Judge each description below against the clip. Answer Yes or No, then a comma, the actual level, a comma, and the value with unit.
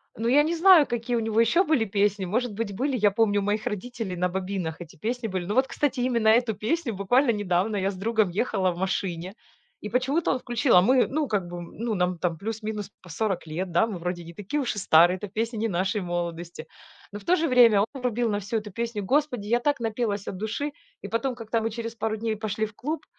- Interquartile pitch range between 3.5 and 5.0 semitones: Yes, average, 4.1 semitones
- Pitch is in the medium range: No, high, 220 Hz